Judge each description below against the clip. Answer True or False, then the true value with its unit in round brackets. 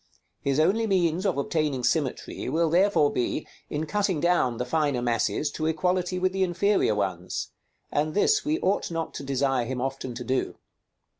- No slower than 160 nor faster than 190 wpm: True (170 wpm)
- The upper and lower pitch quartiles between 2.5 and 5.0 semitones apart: False (5.6 semitones)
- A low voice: False (155 Hz)